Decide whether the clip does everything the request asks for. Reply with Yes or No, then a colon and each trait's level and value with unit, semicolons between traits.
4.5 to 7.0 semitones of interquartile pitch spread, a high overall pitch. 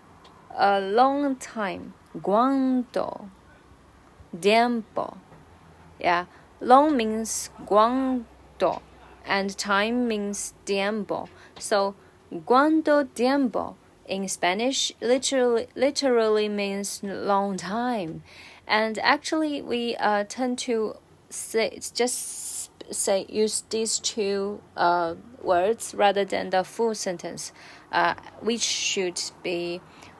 No: average, 4.1 semitones; high, 215 Hz